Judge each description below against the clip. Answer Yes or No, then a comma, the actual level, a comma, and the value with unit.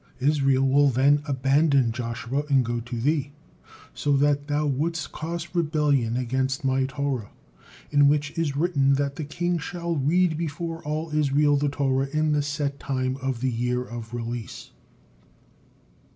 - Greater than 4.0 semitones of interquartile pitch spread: No, narrow, 2.5 semitones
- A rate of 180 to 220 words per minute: No, average, 150 wpm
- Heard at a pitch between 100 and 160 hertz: Yes, medium, 140 Hz